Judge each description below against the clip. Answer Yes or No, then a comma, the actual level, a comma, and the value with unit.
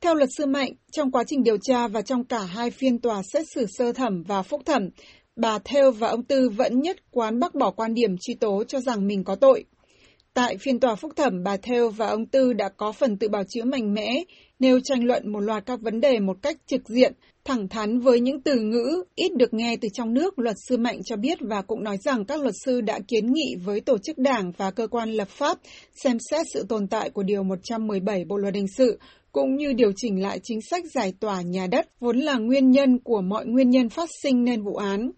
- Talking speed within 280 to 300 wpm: No, average, 245 wpm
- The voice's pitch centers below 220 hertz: No, high, 240 Hz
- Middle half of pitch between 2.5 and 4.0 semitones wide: Yes, average, 3.7 semitones